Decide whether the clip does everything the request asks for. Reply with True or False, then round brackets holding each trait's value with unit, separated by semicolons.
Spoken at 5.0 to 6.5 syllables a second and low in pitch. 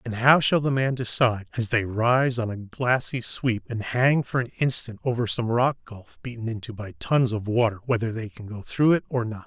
True (5.1 syllables/s; 115 Hz)